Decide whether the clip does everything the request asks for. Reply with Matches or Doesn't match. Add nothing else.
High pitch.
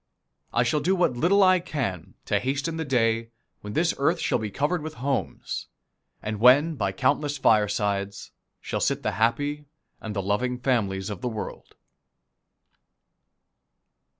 Doesn't match